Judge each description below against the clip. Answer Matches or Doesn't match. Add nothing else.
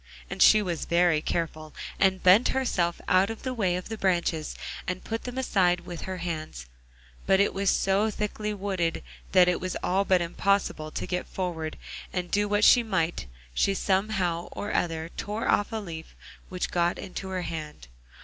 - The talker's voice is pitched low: Doesn't match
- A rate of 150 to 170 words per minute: Doesn't match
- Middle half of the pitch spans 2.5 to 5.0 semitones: Matches